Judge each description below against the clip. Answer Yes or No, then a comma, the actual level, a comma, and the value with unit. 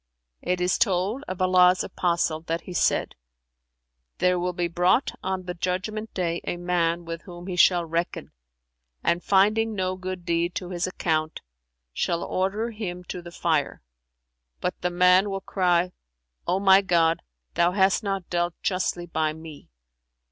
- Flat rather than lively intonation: Yes, narrow, 1.6 semitones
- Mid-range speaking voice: Yes, medium, 180 Hz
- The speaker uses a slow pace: No, average, 155 wpm